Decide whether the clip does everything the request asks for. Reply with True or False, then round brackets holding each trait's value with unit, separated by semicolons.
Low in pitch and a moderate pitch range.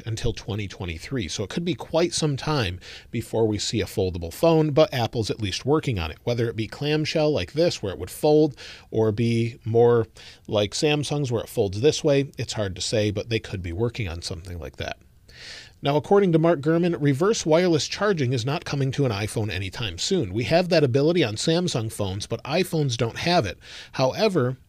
False (120 Hz; 6.4 semitones)